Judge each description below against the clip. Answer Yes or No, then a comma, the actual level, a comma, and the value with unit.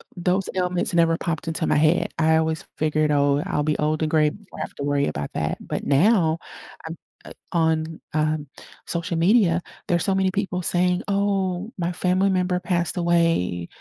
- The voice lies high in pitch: No, medium, 170 Hz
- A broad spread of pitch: No, average, 2.7 semitones